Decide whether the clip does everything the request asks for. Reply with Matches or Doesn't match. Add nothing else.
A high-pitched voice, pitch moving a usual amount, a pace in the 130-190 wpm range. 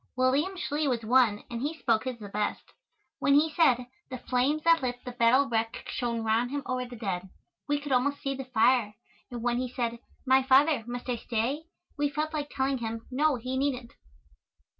Doesn't match